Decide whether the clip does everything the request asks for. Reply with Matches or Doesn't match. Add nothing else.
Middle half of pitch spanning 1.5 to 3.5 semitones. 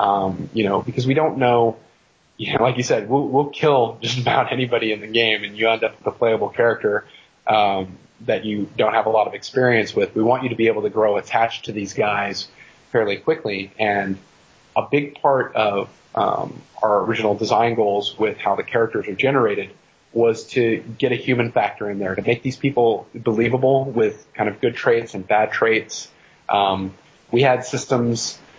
Matches